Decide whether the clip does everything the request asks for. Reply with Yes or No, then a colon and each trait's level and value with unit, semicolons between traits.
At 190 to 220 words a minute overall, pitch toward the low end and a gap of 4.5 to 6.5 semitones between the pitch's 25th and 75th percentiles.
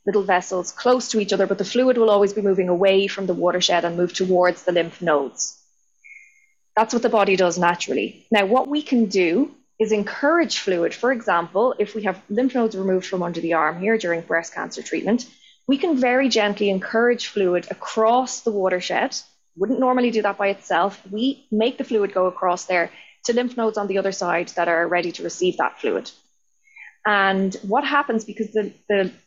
No: average, 195 wpm; high, 205 Hz; average, 4.8 semitones